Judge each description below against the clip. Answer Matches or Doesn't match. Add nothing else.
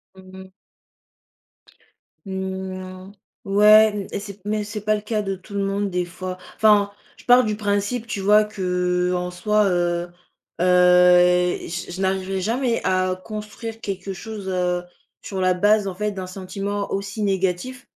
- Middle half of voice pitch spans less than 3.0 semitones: Matches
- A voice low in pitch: Doesn't match